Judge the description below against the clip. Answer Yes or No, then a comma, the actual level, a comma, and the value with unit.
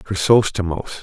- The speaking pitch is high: No, very low, 95 Hz